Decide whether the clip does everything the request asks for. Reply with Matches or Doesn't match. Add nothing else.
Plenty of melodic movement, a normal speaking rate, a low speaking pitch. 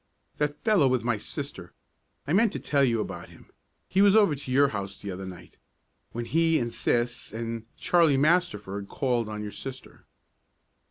Matches